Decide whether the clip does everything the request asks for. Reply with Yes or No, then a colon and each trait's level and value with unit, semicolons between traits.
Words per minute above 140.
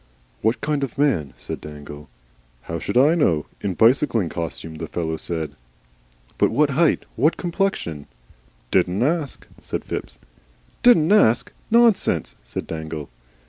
No: slow, 135 wpm